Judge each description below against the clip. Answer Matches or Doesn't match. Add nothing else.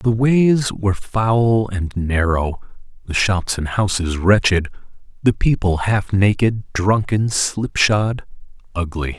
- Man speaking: Matches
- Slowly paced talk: Matches